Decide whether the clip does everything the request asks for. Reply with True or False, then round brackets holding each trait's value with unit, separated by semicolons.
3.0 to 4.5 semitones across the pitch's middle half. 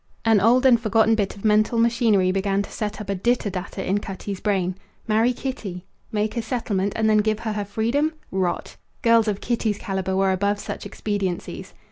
False (2.5 semitones)